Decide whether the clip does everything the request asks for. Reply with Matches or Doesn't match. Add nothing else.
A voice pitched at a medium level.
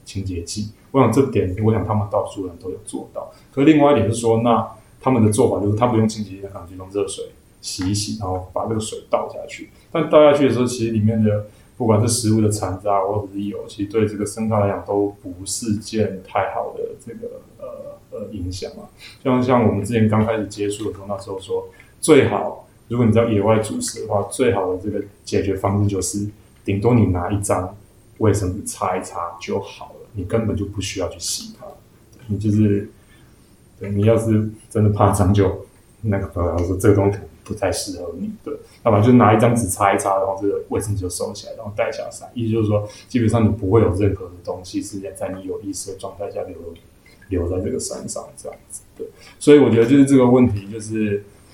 Doesn't match